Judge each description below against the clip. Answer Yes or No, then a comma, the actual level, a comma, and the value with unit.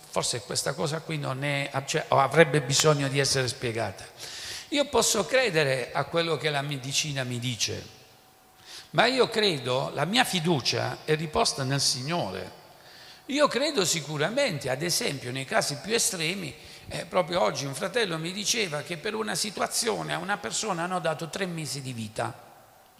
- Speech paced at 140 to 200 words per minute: Yes, average, 160 wpm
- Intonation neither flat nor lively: No, wide, 6.2 semitones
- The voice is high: No, medium, 155 Hz